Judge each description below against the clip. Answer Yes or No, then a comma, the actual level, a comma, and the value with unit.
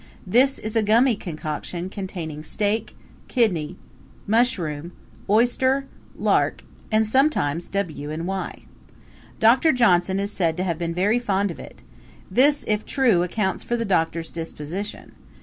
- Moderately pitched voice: No, high, 200 Hz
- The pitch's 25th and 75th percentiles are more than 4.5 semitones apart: Yes, average, 5.3 semitones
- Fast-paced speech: No, slow, 135 wpm